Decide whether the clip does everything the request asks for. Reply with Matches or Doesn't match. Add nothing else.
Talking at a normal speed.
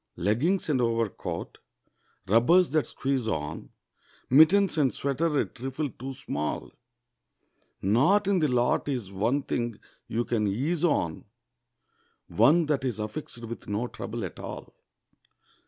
Doesn't match